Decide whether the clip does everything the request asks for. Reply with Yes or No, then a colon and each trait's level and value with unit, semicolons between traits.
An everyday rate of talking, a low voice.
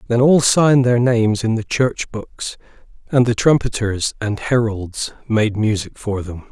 Yes: average, 165 wpm; low, 115 Hz